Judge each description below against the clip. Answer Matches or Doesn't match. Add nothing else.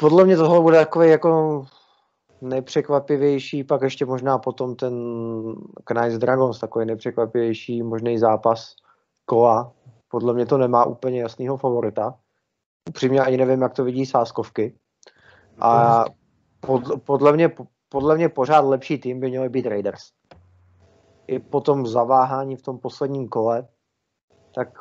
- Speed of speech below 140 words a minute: Matches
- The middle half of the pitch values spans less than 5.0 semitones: Matches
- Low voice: Matches